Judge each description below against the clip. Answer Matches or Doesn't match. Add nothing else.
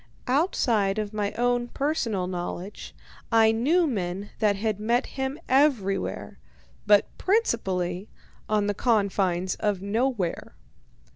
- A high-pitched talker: Matches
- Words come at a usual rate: Doesn't match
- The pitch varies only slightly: Doesn't match